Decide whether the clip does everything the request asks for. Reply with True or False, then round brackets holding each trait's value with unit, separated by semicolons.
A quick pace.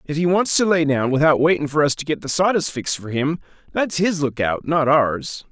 True (240 wpm)